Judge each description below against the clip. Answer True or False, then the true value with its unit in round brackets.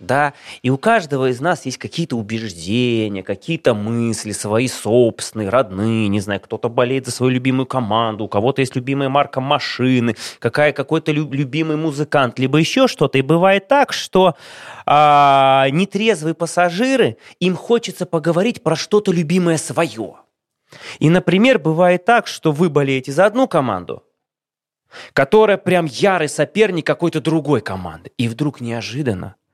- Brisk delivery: False (140 wpm)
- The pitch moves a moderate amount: False (6.1 semitones)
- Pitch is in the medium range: True (145 Hz)